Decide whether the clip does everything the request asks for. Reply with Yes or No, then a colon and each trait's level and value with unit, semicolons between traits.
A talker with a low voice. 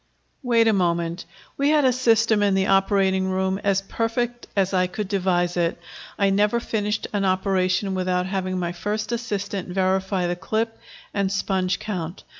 No: high, 195 Hz